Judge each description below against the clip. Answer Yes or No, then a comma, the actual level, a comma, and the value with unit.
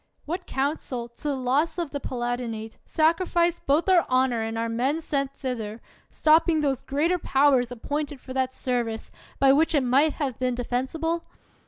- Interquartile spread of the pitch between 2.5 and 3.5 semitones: No, average, 4.0 semitones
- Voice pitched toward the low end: No, very high, 270 Hz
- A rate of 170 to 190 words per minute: Yes, average, 175 wpm